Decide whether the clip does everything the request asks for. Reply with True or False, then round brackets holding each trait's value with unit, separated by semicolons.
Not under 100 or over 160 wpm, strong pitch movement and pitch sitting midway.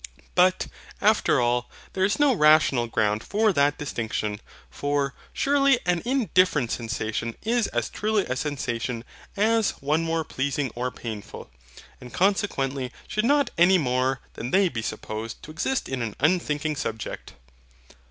True (140 wpm; 7.9 semitones; 145 Hz)